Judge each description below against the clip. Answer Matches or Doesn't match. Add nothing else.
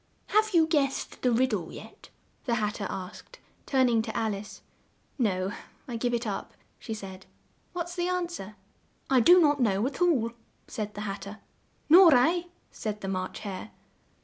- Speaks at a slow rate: Doesn't match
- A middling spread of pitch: Doesn't match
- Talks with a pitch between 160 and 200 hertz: Doesn't match